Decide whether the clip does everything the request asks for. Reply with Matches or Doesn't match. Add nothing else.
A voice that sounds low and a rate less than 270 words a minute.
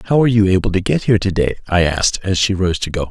Doesn't match